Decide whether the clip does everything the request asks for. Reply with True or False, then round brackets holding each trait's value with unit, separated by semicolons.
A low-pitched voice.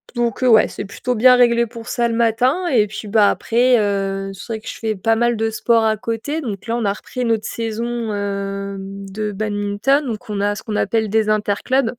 False (220 Hz)